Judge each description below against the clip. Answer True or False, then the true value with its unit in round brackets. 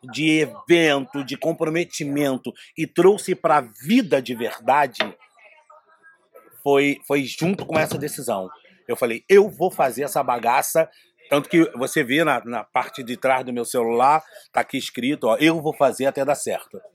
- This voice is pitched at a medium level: True (155 Hz)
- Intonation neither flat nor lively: True (3.8 semitones)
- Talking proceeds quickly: False (165 wpm)